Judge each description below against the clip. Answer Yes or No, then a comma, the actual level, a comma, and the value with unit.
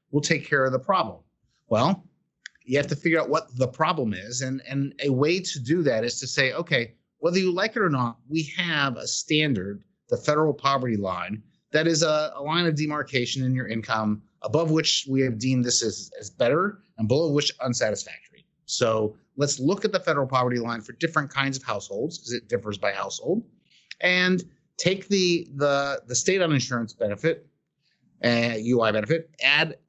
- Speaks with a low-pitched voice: No, medium, 145 Hz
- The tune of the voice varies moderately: Yes, average, 4.7 semitones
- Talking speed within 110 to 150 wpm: No, average, 190 wpm